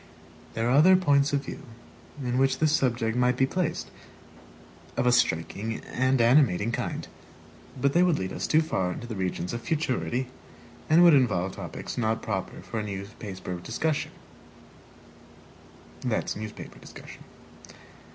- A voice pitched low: Yes, low, 125 Hz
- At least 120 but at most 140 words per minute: Yes, slow, 135 wpm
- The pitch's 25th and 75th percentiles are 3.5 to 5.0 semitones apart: Yes, average, 4.6 semitones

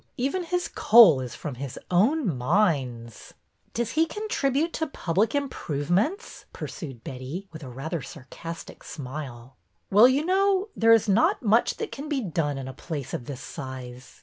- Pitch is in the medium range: Yes, medium, 175 Hz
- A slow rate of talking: No, average, 170 wpm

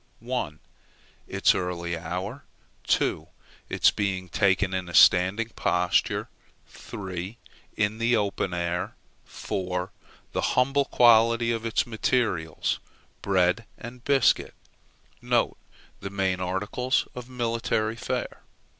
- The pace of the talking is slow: Yes, slow, 105 wpm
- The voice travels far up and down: No, average, 4.4 semitones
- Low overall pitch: Yes, low, 100 Hz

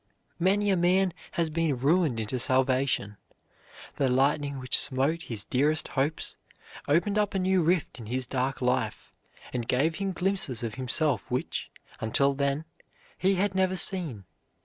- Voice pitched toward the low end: No, medium, 145 Hz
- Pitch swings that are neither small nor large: No, wide, 6.0 semitones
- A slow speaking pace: No, average, 150 wpm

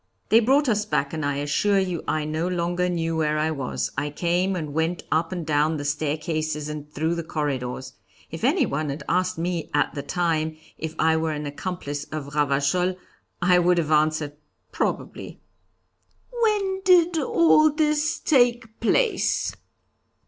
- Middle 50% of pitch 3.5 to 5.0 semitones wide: Yes, average, 3.8 semitones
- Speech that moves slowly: No, average, 160 wpm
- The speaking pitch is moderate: Yes, medium, 160 Hz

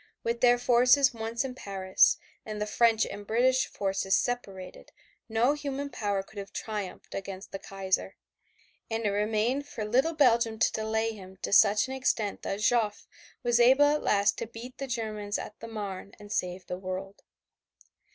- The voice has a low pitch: No, high, 220 Hz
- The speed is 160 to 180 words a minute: Yes, average, 170 wpm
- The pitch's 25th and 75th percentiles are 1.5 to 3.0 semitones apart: No, average, 3.5 semitones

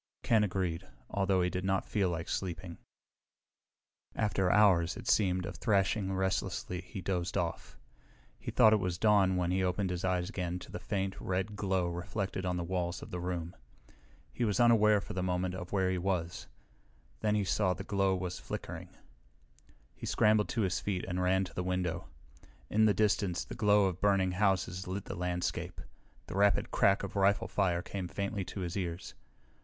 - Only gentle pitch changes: Yes, narrow, 1.9 semitones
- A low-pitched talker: Yes, very low, 95 Hz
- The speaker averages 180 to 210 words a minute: Yes, average, 185 wpm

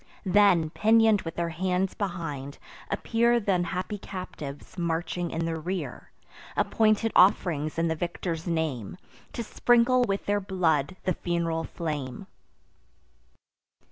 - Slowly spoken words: Yes, slow, 120 wpm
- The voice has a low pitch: No, medium, 175 Hz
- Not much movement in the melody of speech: No, average, 3.8 semitones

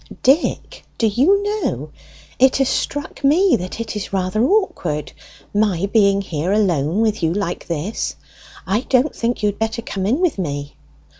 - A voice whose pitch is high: Yes, high, 210 Hz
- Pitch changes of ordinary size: No, wide, 6.2 semitones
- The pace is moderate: Yes, average, 165 wpm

